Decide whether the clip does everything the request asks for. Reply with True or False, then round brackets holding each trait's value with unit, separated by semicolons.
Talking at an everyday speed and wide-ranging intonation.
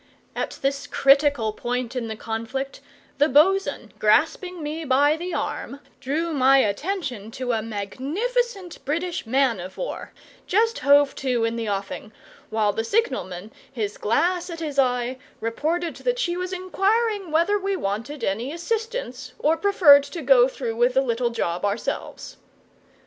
True (150 wpm; 7.1 semitones)